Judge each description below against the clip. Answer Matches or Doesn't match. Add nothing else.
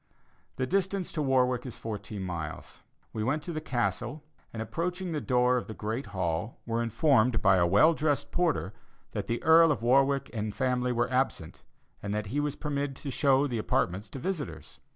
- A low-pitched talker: Matches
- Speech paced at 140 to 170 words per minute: Doesn't match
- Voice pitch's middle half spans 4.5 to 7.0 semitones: Matches